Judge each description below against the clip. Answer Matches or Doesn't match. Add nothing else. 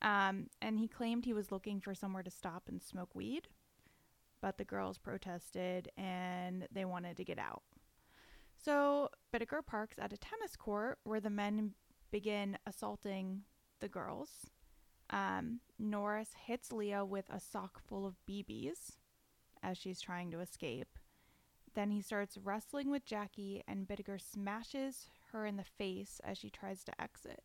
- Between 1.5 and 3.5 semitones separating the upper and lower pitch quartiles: Matches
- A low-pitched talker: Doesn't match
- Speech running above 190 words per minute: Doesn't match